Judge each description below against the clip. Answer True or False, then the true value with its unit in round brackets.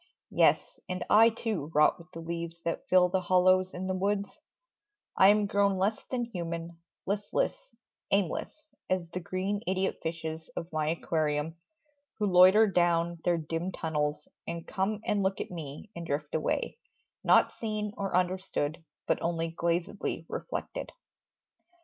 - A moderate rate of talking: True (150 wpm)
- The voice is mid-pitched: True (180 Hz)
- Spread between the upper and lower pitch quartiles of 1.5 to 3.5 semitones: True (3.1 semitones)